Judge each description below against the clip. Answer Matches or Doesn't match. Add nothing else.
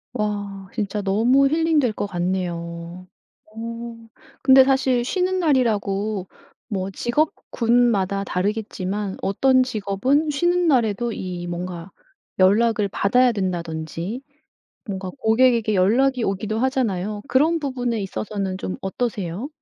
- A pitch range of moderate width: Matches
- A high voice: Matches